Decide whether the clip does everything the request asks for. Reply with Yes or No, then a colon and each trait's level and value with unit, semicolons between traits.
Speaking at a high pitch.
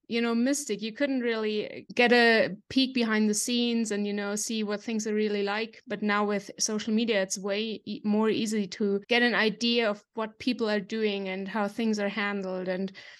Yes: high, 215 Hz